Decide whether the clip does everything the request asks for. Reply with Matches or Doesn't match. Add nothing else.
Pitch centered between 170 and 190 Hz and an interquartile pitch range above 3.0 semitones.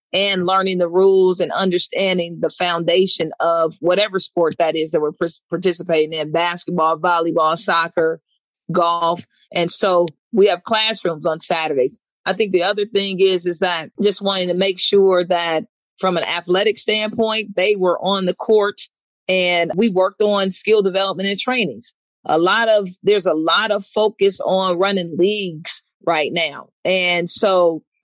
Doesn't match